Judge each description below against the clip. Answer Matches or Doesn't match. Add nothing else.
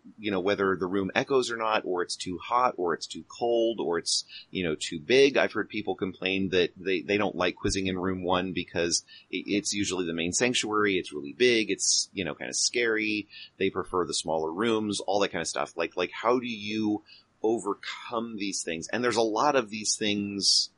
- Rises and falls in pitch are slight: Doesn't match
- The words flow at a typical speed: Doesn't match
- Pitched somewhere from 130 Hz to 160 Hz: Doesn't match